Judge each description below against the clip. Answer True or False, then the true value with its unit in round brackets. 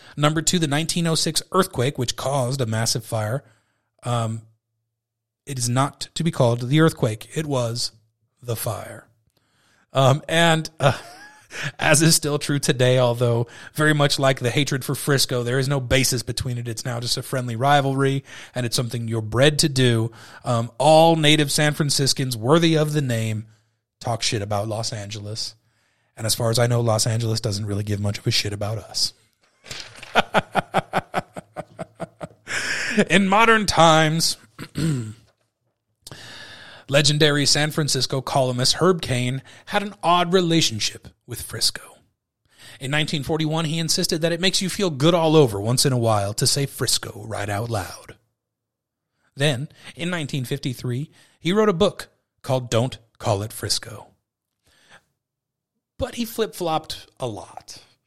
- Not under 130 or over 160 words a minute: True (150 wpm)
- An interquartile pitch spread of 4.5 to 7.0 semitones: True (5.0 semitones)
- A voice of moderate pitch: False (130 Hz)